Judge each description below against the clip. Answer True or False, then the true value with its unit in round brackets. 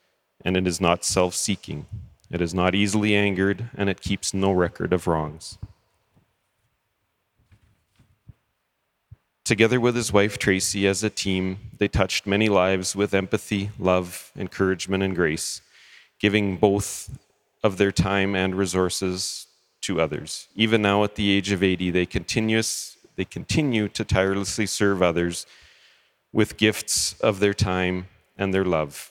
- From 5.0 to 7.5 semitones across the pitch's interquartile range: False (2.4 semitones)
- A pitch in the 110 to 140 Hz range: False (100 Hz)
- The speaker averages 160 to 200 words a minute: False (135 wpm)